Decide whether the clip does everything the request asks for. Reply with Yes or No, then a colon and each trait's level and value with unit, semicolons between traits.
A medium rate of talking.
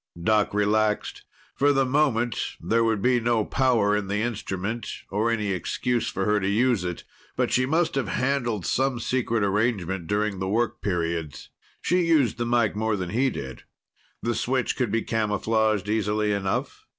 Yes: average, 170 wpm